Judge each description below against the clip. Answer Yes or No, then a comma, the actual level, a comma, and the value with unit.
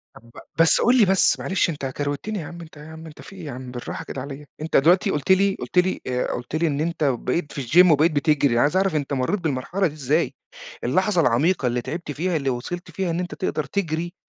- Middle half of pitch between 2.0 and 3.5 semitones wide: No, average, 4.5 semitones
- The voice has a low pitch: No, medium, 155 Hz